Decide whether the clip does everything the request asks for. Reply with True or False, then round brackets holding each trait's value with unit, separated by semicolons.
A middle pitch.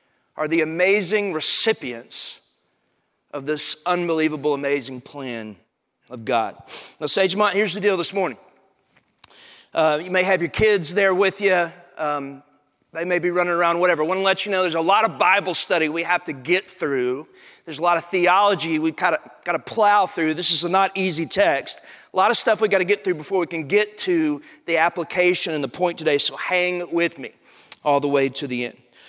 True (175 Hz)